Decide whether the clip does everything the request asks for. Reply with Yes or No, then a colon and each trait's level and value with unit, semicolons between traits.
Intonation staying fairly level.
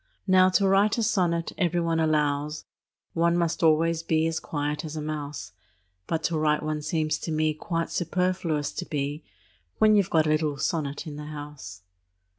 Yes: narrow, 2.2 semitones